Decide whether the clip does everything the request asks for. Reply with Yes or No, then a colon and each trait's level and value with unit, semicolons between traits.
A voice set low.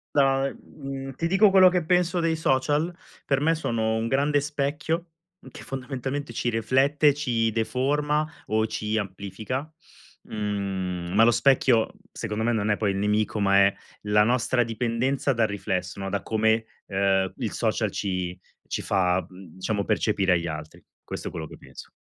Yes: low, 115 Hz